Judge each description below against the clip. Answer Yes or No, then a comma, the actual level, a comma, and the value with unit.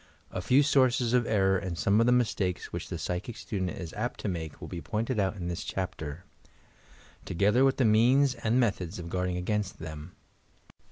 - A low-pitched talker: Yes, low, 100 Hz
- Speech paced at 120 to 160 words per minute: No, average, 200 wpm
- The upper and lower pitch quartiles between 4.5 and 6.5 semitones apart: Yes, average, 5.1 semitones